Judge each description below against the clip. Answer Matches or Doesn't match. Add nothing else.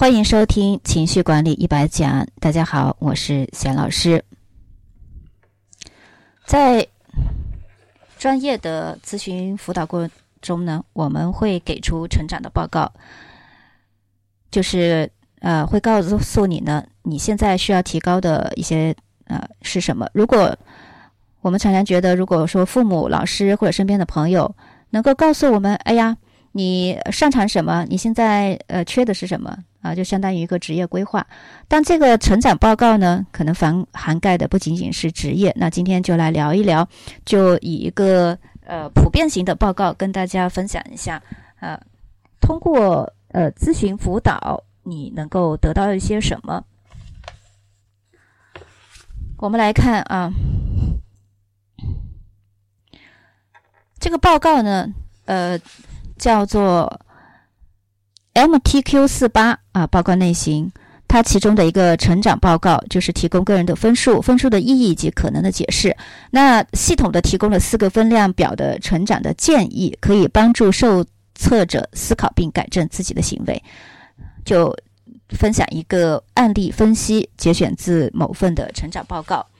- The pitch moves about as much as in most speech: Doesn't match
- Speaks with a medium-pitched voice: Matches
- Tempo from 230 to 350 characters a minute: Doesn't match